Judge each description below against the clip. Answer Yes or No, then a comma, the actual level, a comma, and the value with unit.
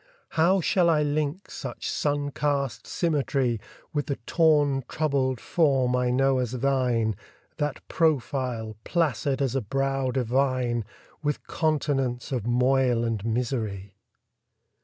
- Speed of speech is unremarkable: No, slow, 120 wpm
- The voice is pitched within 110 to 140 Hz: Yes, low, 135 Hz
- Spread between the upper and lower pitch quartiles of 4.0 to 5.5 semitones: No, average, 3.1 semitones